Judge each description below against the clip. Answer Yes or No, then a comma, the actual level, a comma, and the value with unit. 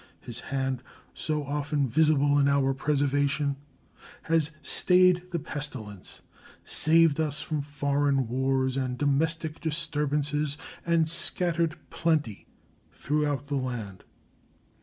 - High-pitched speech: No, medium, 145 Hz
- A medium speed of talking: No, slow, 105 wpm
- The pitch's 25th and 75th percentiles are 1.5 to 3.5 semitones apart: Yes, narrow, 2.4 semitones